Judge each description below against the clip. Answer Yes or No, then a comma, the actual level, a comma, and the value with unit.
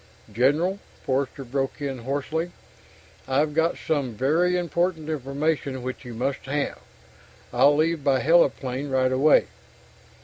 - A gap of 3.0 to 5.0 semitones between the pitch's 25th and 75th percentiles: Yes, average, 3.3 semitones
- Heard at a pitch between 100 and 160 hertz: Yes, medium, 140 Hz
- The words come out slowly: Yes, slow, 130 wpm